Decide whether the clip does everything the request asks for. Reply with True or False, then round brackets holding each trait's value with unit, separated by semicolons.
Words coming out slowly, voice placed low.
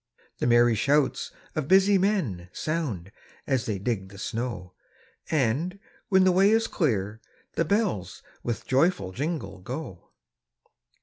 True (130 wpm; 130 Hz)